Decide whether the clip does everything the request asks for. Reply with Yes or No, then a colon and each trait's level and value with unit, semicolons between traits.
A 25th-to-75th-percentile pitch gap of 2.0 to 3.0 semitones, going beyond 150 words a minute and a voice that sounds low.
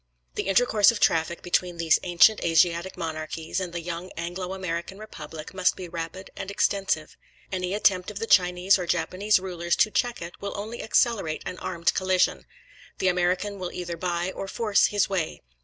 No: narrow, 2.4 semitones; average, 175 wpm; medium, 180 Hz